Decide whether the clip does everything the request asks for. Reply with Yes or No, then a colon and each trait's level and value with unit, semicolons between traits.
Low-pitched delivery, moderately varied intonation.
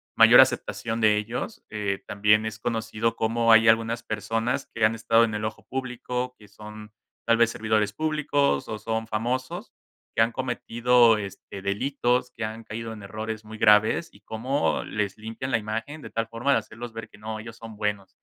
No: low, 115 Hz; narrow, 1.6 semitones